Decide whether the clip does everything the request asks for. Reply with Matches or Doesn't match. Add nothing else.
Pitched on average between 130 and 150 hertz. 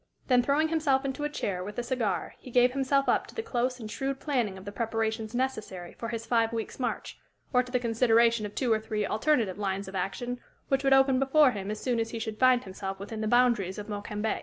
Doesn't match